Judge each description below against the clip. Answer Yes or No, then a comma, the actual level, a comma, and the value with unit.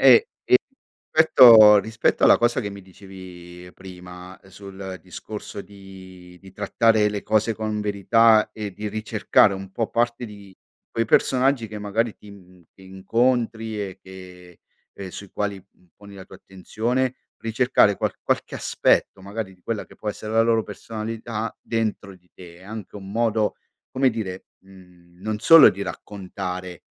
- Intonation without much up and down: No, average, 3.0 semitones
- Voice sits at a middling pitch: No, low, 105 Hz